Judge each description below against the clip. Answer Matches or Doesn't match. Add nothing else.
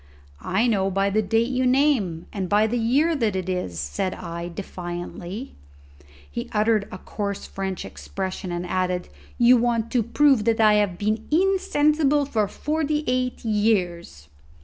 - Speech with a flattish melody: Doesn't match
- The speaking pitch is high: Matches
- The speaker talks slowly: Doesn't match